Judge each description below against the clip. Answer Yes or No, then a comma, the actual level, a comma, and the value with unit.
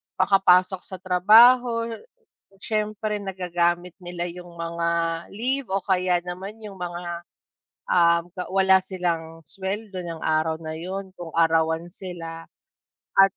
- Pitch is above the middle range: No, medium, 180 Hz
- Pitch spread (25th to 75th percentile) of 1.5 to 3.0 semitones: Yes, narrow, 2.4 semitones